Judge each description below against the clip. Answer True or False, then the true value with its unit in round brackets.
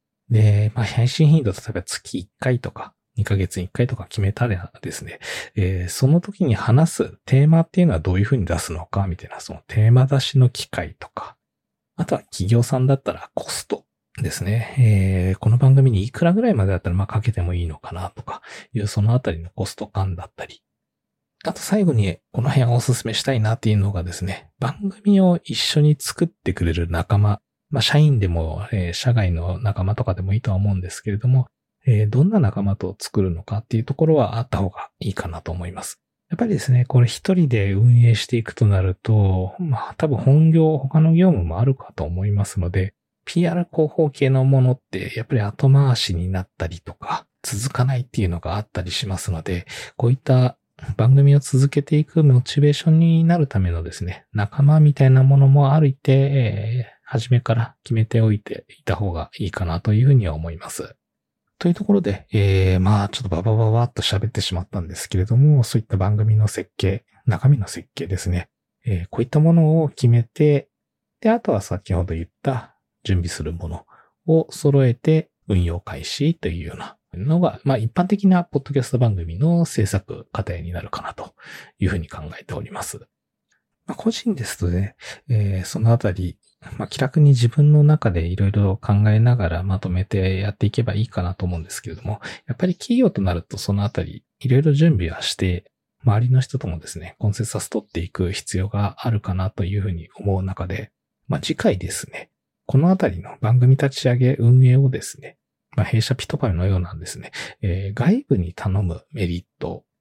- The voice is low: True (110 Hz)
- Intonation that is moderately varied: False (6.1 semitones)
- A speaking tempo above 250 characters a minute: True (380 characters per minute)